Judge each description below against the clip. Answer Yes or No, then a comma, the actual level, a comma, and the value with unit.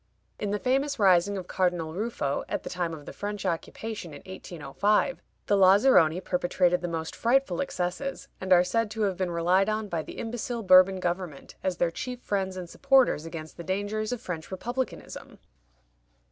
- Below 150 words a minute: No, average, 175 wpm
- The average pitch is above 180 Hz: Yes, high, 190 Hz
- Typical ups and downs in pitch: Yes, average, 3.8 semitones